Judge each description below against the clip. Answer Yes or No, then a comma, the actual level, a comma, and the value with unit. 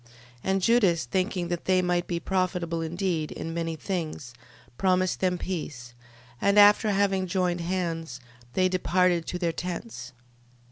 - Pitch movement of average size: No, narrow, 2.1 semitones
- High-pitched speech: No, medium, 180 Hz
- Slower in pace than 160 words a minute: Yes, average, 145 wpm